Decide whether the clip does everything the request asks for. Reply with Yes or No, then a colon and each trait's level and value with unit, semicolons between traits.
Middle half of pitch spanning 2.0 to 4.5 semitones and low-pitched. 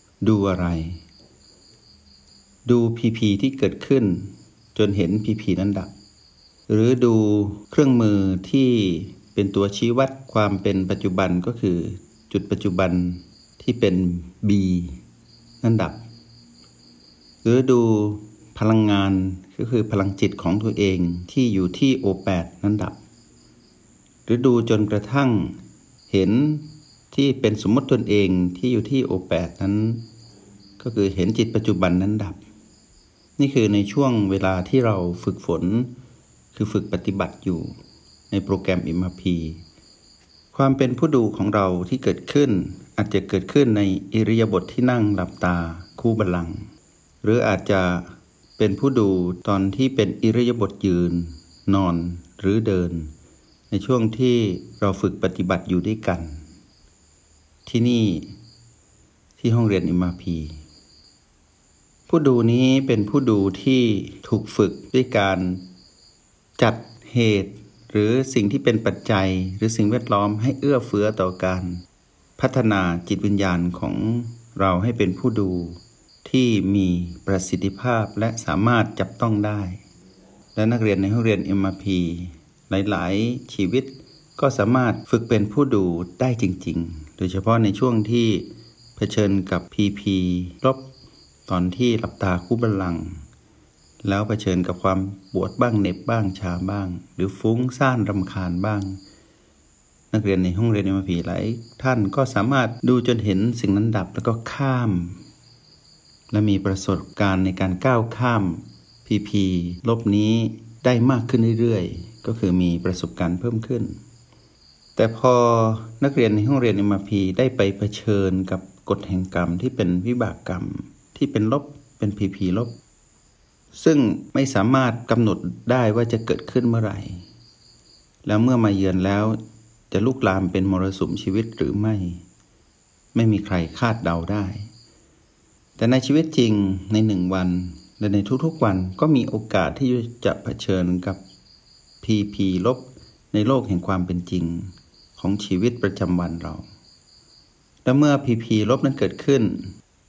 Yes: average, 3.8 semitones; low, 100 Hz